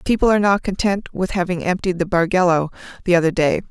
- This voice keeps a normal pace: No, fast, 210 wpm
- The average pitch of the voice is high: No, medium, 180 Hz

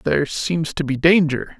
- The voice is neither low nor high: Yes, medium, 150 Hz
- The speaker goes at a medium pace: Yes, average, 190 wpm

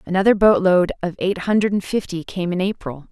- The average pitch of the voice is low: No, medium, 185 Hz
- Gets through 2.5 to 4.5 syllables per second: No, 5.6 syllables/s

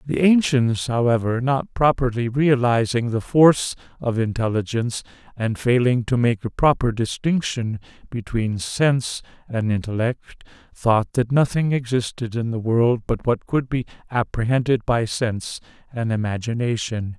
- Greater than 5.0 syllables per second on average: No, 4.6 syllables/s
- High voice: No, low, 120 Hz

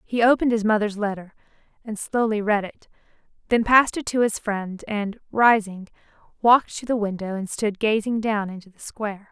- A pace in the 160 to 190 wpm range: Yes, average, 180 wpm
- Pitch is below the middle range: No, high, 215 Hz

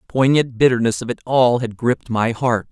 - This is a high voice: No, low, 120 Hz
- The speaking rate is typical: No, fast, 220 wpm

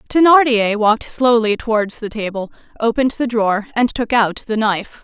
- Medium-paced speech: Yes, average, 165 wpm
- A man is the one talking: No, female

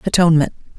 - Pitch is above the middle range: No, medium, 165 Hz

